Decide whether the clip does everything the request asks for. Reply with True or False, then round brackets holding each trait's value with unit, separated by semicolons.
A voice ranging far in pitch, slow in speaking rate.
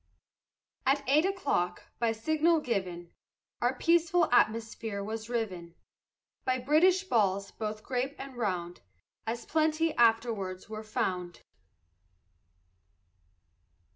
True (6.4 semitones; 100 wpm)